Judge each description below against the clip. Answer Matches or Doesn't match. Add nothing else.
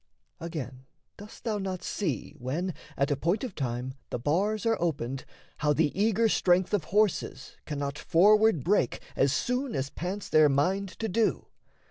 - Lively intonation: Matches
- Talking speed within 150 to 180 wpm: Matches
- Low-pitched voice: Doesn't match